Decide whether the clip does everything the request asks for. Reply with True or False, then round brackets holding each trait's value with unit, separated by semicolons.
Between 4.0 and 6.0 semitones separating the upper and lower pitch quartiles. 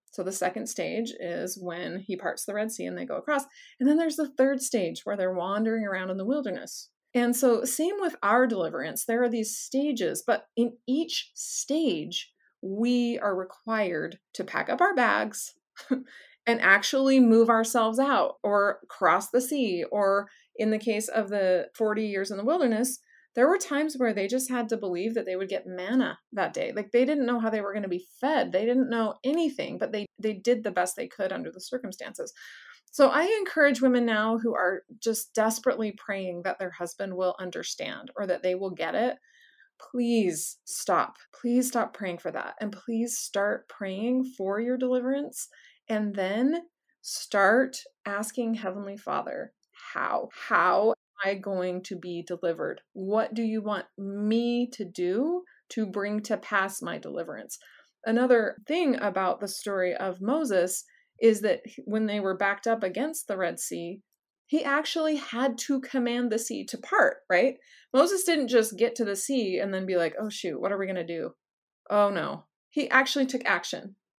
True (4.7 semitones)